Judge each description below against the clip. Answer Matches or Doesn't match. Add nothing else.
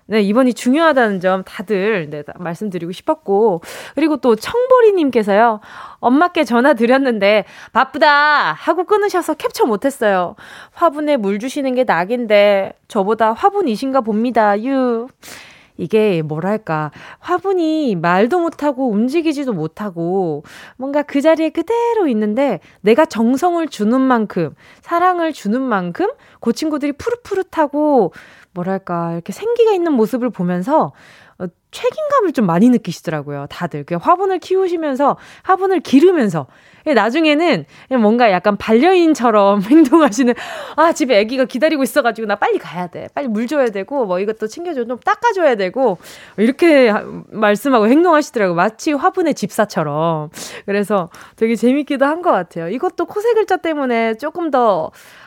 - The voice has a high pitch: Matches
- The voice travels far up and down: Matches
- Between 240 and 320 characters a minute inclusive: Doesn't match